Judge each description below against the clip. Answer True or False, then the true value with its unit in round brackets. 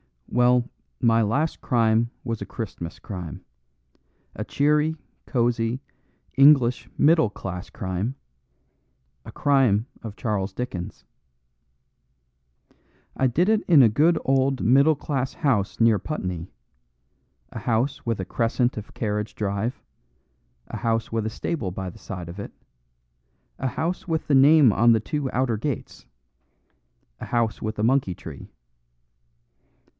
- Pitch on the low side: True (115 Hz)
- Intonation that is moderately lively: True (4.5 semitones)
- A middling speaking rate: False (130 wpm)